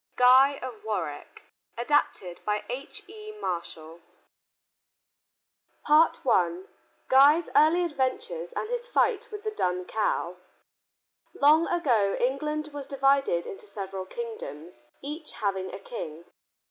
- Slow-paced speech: Yes, slow, 110 wpm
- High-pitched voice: Yes, very high, 260 Hz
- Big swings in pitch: Yes, wide, 8.5 semitones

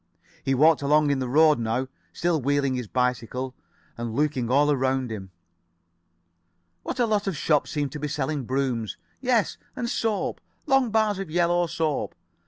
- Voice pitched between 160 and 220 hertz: No, medium, 145 Hz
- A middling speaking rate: Yes, average, 165 wpm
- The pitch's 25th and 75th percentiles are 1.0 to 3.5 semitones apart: No, average, 5.1 semitones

